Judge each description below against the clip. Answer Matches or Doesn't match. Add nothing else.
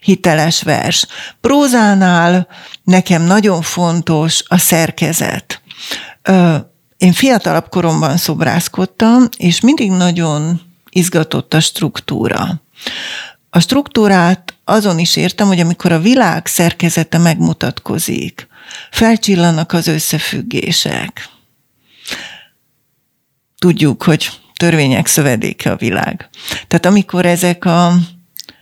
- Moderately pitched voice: Matches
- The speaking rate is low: Matches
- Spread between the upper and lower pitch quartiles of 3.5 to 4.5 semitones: Doesn't match